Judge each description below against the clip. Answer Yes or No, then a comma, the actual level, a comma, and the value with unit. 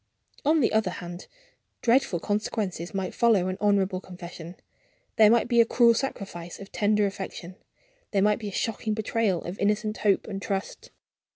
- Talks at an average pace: Yes, average, 165 wpm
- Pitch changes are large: No, average, 3.0 semitones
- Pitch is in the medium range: No, high, 205 Hz